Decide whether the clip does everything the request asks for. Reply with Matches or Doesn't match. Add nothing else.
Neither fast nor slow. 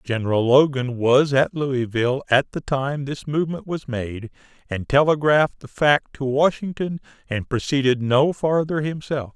Matches